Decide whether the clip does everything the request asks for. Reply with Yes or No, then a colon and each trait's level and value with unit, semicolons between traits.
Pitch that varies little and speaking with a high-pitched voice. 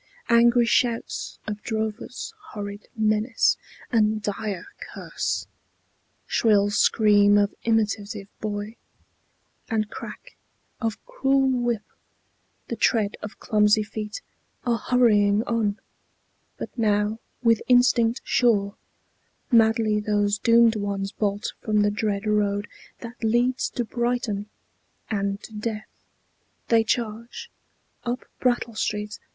Yes: narrow, 2.1 semitones; high, 215 Hz